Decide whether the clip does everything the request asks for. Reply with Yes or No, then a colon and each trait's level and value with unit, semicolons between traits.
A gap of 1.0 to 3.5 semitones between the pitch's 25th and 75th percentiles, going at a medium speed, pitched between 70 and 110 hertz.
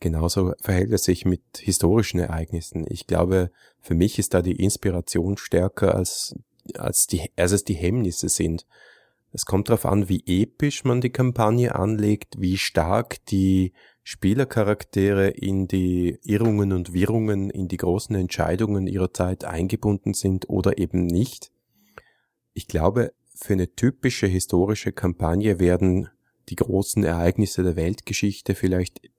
Yes: narrow, 2.6 semitones; average, 140 wpm; very low, 95 Hz